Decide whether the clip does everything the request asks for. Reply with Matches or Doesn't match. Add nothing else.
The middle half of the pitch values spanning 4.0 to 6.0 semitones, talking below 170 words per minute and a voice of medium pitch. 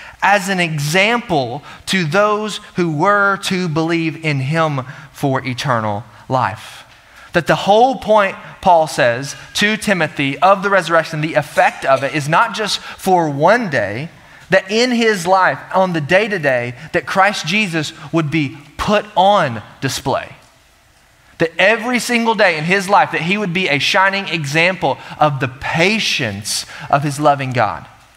Matches